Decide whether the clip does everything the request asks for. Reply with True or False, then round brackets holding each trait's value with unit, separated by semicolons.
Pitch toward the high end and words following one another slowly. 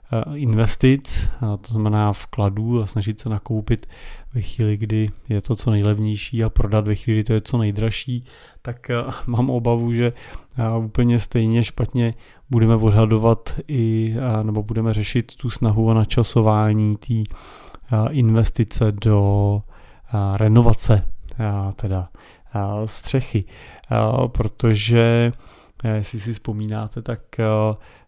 False (110 Hz; 110 wpm)